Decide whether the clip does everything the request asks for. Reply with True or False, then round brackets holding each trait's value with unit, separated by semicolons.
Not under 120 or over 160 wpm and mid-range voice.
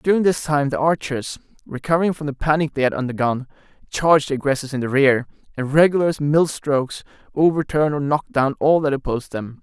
False (195 wpm; 145 Hz)